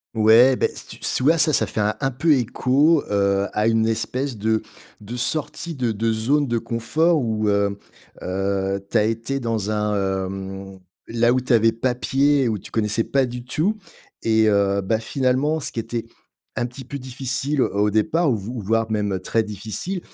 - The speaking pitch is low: Yes, low, 115 Hz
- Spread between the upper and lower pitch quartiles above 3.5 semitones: Yes, average, 3.9 semitones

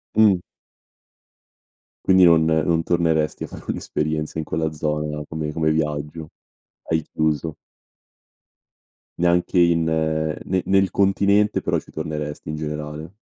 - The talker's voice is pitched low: Yes, very low, 80 Hz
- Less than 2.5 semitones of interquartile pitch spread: Yes, narrow, 2.1 semitones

